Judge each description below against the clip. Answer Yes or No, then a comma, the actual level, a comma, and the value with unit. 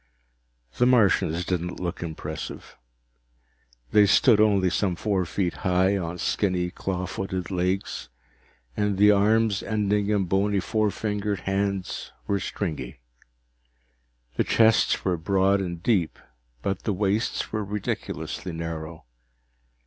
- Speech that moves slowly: Yes, slow, 120 wpm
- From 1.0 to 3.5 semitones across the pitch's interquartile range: Yes, narrow, 2.6 semitones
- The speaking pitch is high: No, very low, 95 Hz